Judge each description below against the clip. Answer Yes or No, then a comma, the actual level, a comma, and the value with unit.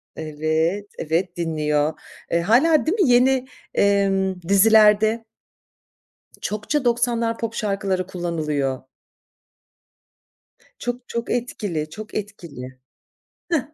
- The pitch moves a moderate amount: No, wide, 6.2 semitones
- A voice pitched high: Yes, high, 200 Hz